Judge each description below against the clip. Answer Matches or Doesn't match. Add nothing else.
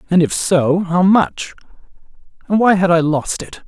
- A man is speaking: Matches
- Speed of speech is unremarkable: Matches